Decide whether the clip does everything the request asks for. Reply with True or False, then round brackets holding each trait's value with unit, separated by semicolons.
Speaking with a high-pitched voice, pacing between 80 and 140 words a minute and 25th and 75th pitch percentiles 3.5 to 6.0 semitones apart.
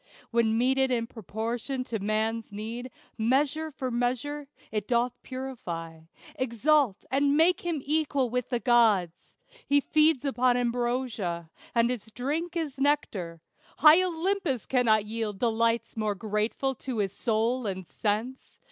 True (245 Hz; 135 wpm; 3.8 semitones)